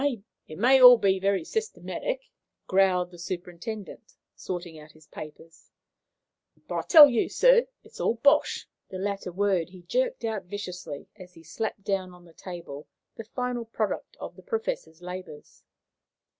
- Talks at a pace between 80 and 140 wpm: No, average, 155 wpm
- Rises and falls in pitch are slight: No, average, 5.2 semitones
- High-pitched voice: Yes, high, 195 Hz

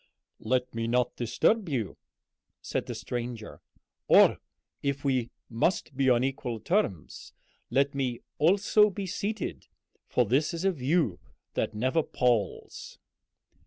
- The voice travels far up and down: Yes, wide, 5.7 semitones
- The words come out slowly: Yes, slow, 125 wpm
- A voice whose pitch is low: Yes, low, 130 Hz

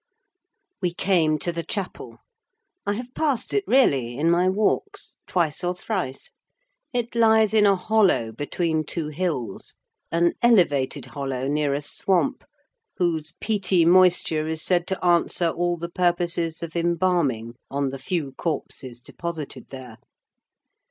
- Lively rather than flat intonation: No, average, 4.2 semitones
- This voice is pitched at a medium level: Yes, medium, 170 Hz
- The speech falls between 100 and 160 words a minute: Yes, average, 140 wpm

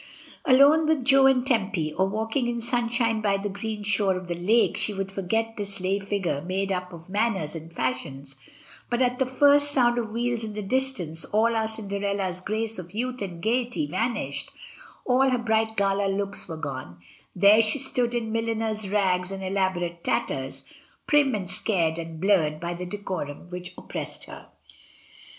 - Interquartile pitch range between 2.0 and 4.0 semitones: No, average, 4.4 semitones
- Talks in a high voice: Yes, high, 205 Hz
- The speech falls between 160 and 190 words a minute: Yes, average, 175 wpm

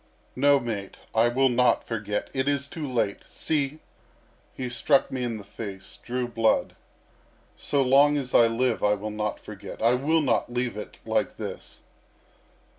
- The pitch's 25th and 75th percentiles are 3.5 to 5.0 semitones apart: Yes, average, 3.9 semitones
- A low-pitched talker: Yes, low, 120 Hz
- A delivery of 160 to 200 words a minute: Yes, average, 165 wpm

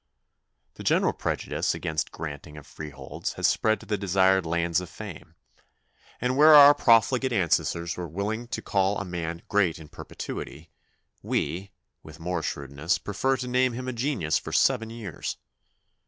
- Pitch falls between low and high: No, very low, 95 Hz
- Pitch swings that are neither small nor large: No, wide, 6.2 semitones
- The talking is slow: No, average, 165 wpm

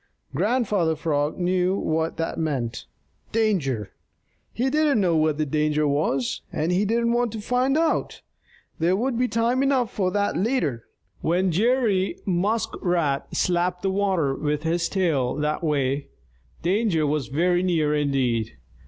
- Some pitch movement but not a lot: No, wide, 5.9 semitones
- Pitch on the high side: No, medium, 175 Hz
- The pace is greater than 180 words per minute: No, average, 145 wpm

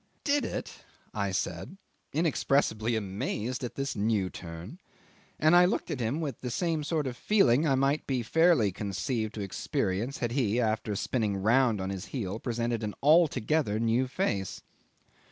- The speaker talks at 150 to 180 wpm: Yes, average, 160 wpm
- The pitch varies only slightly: No, wide, 5.4 semitones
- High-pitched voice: No, low, 120 Hz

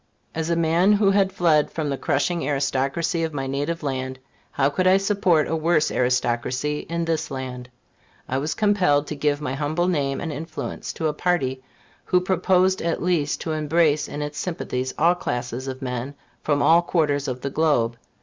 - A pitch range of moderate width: Yes, average, 3.8 semitones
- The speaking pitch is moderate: Yes, medium, 150 Hz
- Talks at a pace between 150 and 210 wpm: Yes, average, 185 wpm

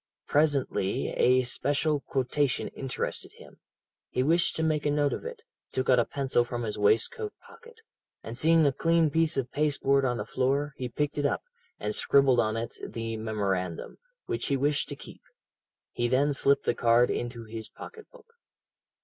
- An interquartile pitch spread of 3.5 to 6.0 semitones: Yes, average, 3.8 semitones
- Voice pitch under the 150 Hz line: Yes, low, 135 Hz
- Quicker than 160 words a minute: Yes, average, 180 wpm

